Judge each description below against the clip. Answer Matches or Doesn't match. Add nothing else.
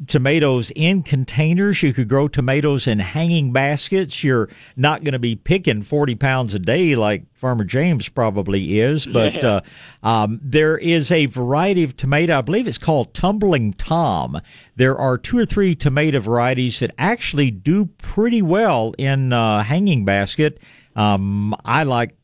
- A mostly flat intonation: Doesn't match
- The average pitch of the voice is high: Doesn't match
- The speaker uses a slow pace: Doesn't match